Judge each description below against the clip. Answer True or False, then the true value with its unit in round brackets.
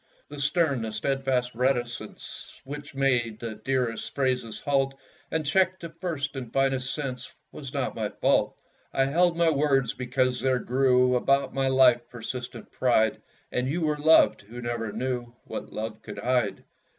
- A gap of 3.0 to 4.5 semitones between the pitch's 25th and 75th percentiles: False (2.5 semitones)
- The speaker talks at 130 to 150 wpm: False (160 wpm)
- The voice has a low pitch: True (130 Hz)